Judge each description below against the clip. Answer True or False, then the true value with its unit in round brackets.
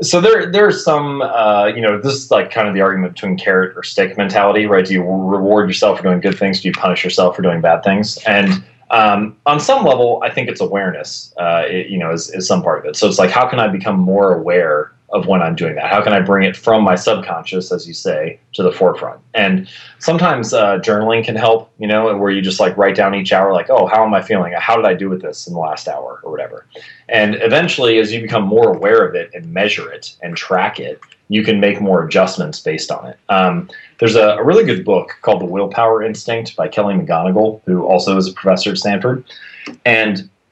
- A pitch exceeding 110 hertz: False (105 Hz)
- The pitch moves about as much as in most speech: True (3.4 semitones)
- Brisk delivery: True (240 wpm)